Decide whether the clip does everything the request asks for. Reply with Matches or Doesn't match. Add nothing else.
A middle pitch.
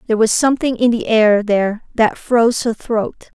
Doesn't match